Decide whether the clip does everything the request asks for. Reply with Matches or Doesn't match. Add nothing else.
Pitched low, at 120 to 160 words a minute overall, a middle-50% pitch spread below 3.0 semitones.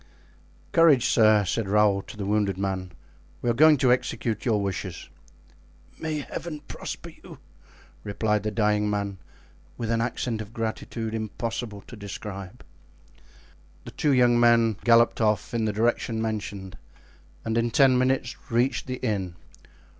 Matches